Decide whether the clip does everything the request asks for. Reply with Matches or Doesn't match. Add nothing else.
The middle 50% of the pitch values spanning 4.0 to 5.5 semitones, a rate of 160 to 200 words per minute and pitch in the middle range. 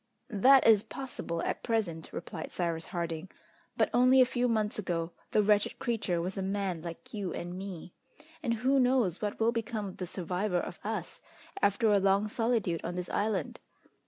Doesn't match